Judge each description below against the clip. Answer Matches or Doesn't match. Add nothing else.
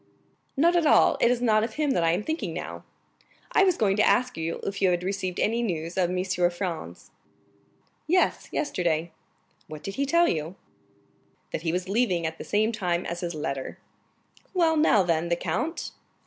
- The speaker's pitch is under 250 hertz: Matches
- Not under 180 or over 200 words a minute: Matches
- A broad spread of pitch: Matches